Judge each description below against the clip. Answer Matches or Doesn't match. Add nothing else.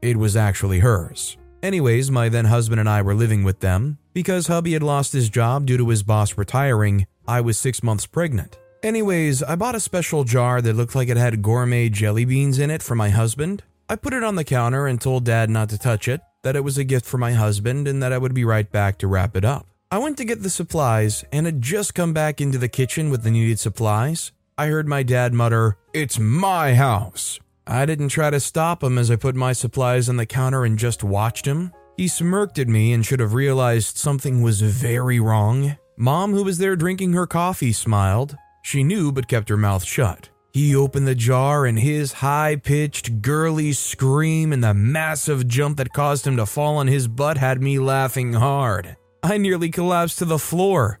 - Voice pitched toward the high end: Doesn't match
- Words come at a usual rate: Doesn't match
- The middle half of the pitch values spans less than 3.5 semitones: Doesn't match